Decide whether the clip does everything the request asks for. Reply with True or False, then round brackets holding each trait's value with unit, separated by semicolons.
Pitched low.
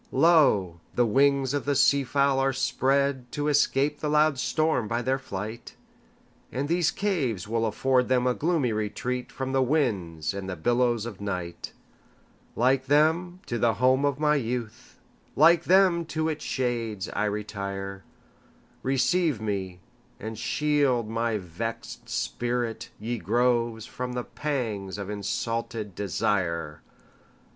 True (125 Hz)